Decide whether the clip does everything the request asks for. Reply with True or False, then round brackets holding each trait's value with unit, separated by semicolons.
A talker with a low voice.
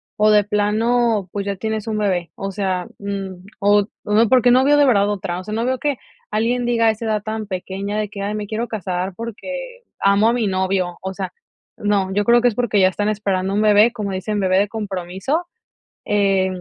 False (205 Hz)